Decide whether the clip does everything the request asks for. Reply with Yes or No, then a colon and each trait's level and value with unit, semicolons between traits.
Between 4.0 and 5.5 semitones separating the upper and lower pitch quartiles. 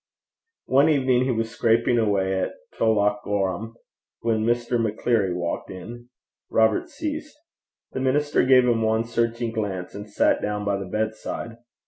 No: average, 2.8 semitones